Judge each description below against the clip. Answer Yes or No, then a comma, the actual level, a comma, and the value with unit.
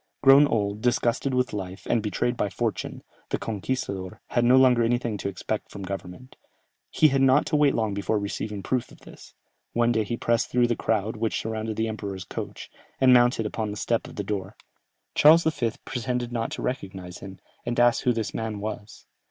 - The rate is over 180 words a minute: Yes, average, 195 wpm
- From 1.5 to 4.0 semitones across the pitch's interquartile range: Yes, average, 3.2 semitones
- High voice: No, low, 115 Hz